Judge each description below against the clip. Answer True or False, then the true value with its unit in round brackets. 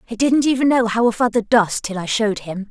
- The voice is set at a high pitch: True (225 Hz)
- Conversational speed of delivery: False (265 wpm)